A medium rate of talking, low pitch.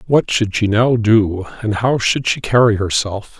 Yes: average, 195 wpm; low, 110 Hz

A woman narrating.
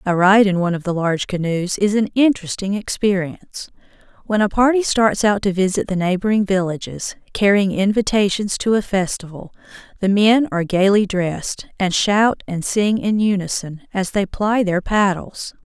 Yes: female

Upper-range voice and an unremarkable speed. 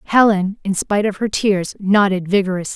Yes: high, 195 Hz; average, 175 wpm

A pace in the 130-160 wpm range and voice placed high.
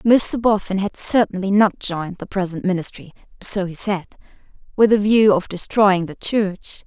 Yes: average, 150 wpm; high, 195 Hz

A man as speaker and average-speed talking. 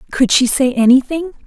No: female; average, 165 wpm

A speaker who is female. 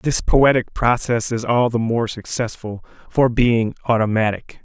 No: male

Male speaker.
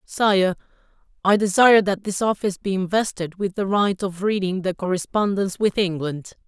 Yes: male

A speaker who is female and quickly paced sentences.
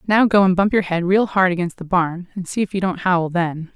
Yes: female; fast, 290 wpm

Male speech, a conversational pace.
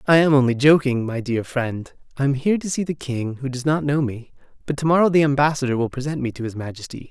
No: male; fast, 255 wpm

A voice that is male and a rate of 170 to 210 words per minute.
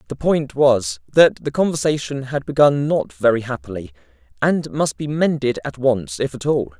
Yes: male; average, 175 wpm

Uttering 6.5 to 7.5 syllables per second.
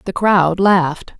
No: 3.9 syllables/s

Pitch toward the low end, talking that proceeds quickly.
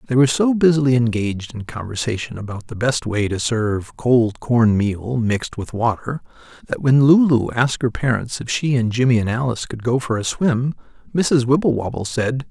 No: low, 120 Hz; average, 185 wpm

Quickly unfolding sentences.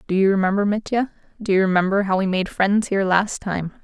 Yes: fast, 220 wpm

